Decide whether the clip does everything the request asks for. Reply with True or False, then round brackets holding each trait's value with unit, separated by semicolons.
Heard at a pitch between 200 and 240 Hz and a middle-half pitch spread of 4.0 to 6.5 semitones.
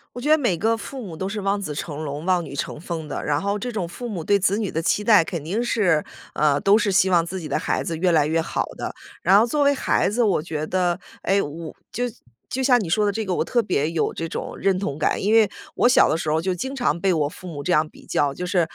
False (185 Hz; 4.7 semitones)